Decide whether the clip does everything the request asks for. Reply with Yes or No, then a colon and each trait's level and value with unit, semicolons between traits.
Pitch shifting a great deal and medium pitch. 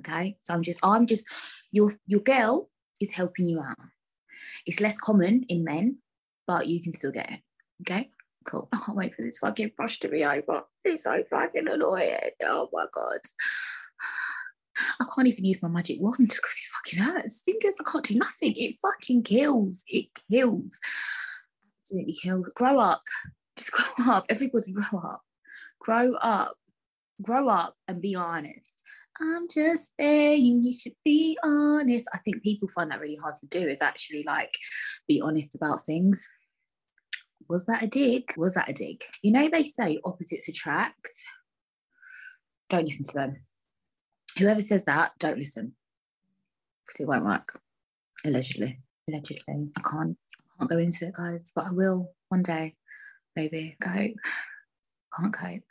No: wide, 7.2 semitones; high, 200 Hz